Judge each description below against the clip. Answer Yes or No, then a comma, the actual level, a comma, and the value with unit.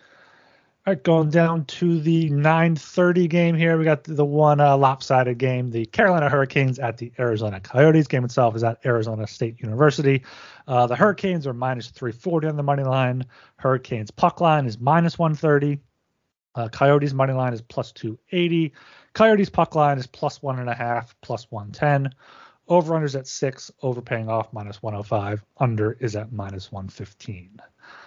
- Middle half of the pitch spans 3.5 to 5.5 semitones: Yes, average, 5.0 semitones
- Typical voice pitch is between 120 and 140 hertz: Yes, low, 135 Hz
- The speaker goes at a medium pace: Yes, average, 165 wpm